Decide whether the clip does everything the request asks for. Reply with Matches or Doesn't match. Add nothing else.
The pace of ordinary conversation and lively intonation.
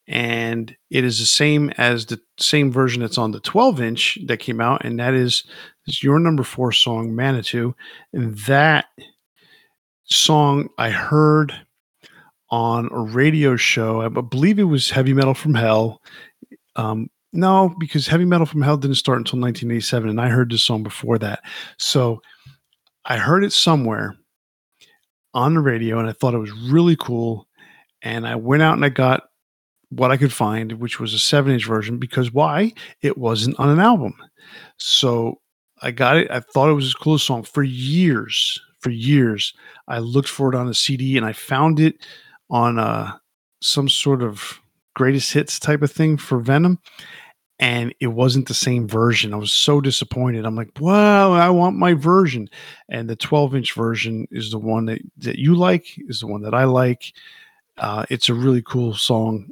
Doesn't match